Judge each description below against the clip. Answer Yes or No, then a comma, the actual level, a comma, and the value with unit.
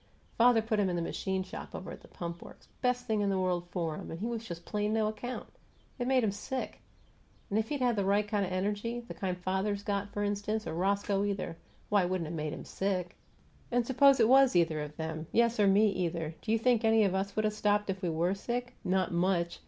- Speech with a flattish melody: No, average, 3.5 semitones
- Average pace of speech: No, fast, 245 wpm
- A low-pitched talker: No, high, 200 Hz